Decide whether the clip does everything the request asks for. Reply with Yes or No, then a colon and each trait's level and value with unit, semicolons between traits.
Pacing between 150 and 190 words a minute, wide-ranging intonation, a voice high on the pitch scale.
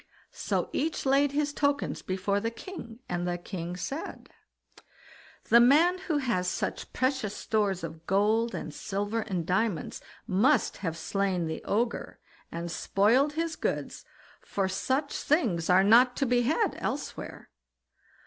No: average, 140 wpm; wide, 6.8 semitones; high, 220 Hz